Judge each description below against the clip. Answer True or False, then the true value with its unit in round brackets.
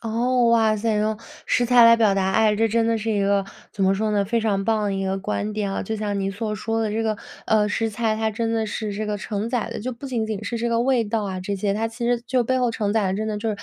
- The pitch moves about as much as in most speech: False (1.9 semitones)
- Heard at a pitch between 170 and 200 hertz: False (220 Hz)